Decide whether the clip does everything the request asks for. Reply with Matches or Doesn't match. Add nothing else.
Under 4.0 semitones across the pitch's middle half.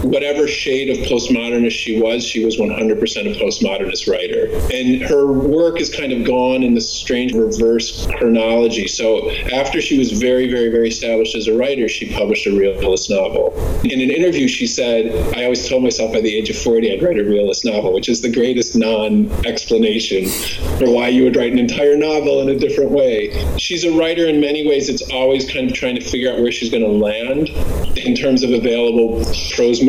Doesn't match